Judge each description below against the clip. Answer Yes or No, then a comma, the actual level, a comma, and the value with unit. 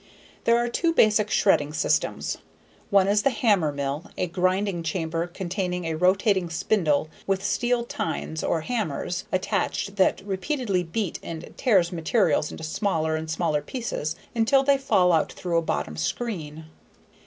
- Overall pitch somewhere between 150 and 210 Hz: Yes, medium, 185 Hz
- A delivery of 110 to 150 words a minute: Yes, average, 145 wpm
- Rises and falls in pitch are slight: No, average, 4.7 semitones